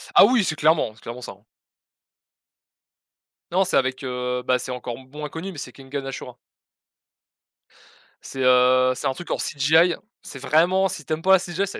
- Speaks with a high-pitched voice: No, medium, 140 Hz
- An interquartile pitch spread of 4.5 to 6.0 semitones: Yes, average, 5.0 semitones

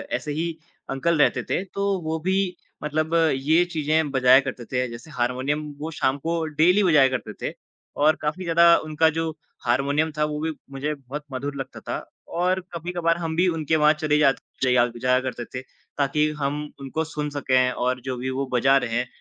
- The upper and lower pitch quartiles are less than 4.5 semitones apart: Yes, average, 3.5 semitones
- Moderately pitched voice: Yes, medium, 150 Hz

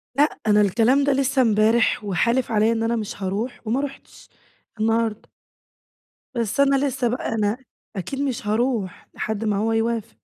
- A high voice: Yes, high, 225 Hz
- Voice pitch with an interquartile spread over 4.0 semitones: No, average, 3.4 semitones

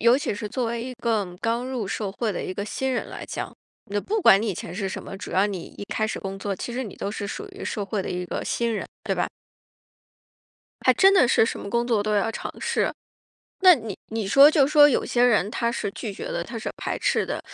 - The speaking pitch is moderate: No, high, 225 Hz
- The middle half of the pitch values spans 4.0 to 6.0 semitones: No, average, 3.5 semitones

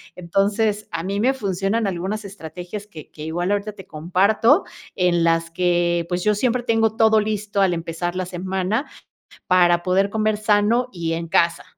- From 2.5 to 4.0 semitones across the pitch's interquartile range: Yes, average, 3.4 semitones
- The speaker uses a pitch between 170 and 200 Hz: Yes, high, 190 Hz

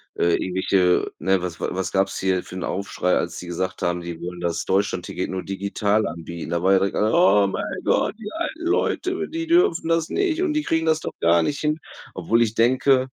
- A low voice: Yes, low, 100 Hz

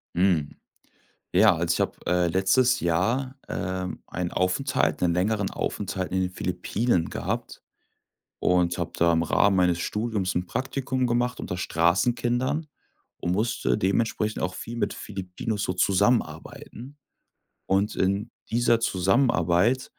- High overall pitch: No, very low, 95 Hz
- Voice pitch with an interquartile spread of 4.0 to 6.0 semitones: Yes, average, 4.7 semitones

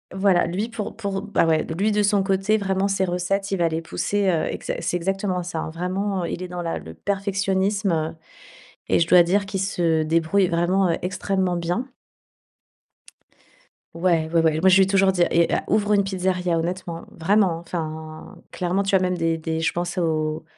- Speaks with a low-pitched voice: No, medium, 180 Hz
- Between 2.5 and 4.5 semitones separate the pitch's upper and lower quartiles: Yes, average, 2.8 semitones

